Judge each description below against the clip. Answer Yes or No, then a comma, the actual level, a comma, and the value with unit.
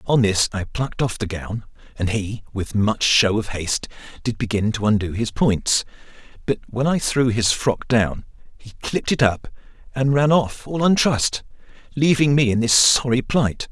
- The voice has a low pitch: Yes, low, 115 Hz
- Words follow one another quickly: No, average, 185 wpm